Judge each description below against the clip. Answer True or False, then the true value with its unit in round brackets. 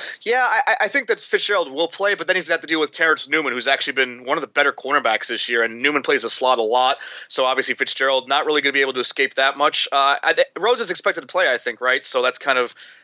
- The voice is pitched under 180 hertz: True (140 Hz)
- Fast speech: True (290 wpm)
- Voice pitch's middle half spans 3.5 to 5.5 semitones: True (4.3 semitones)